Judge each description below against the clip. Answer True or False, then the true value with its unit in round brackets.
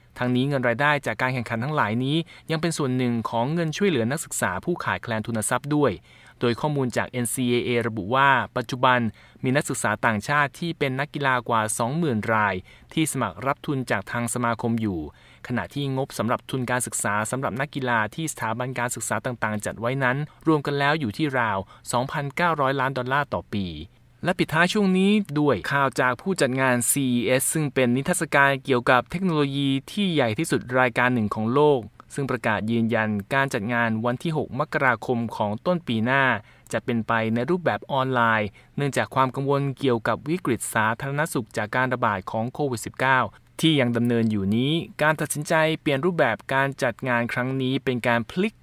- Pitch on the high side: False (130 Hz)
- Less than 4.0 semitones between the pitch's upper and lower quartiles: True (3.6 semitones)